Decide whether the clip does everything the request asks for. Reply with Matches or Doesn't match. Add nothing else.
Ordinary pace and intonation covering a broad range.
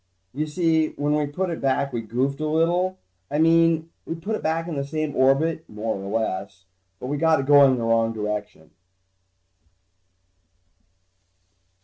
Matches